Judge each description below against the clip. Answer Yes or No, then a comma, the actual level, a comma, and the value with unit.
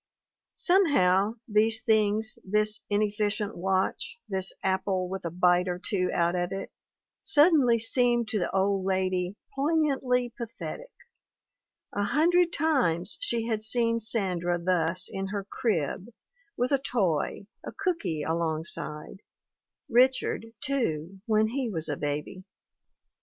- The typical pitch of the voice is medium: No, high, 205 Hz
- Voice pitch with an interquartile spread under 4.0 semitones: No, average, 4.8 semitones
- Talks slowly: Yes, slow, 125 wpm